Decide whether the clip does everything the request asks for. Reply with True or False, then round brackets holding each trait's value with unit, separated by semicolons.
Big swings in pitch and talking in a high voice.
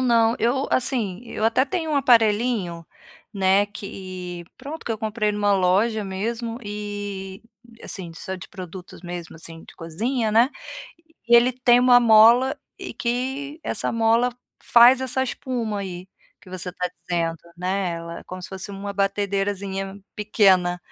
False (4.2 semitones; 205 Hz)